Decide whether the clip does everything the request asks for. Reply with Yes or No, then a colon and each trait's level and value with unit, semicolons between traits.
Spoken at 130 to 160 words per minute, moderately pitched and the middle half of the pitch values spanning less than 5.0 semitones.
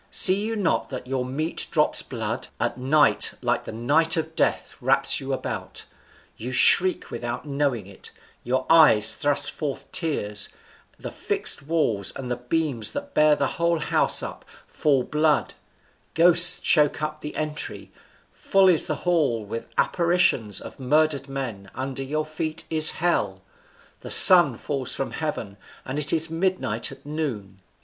Yes: average, 155 wpm; medium, 150 Hz; average, 4.4 semitones